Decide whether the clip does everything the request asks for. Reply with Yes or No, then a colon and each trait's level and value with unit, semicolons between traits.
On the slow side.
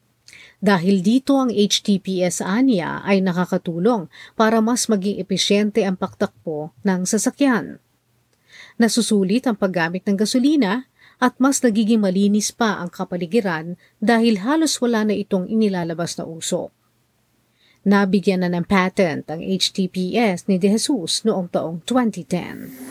No: average, 125 wpm